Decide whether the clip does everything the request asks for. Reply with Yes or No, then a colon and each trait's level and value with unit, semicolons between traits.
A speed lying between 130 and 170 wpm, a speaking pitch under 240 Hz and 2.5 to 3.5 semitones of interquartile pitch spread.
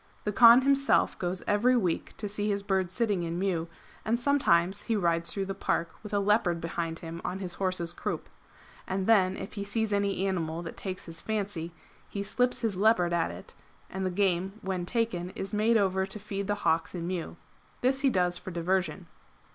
No: average, 200 wpm; high, 190 Hz; average, 3.1 semitones